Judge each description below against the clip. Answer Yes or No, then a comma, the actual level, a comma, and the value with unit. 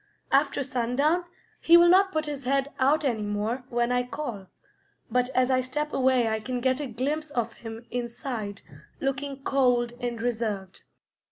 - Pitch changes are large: No, average, 3.0 semitones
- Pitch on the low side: No, very high, 255 Hz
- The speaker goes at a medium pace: Yes, average, 165 wpm